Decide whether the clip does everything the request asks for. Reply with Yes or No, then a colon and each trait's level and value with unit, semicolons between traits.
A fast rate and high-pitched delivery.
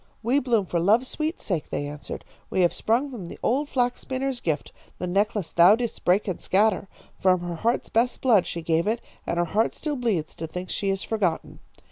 Yes: fast, 210 wpm; high, 205 Hz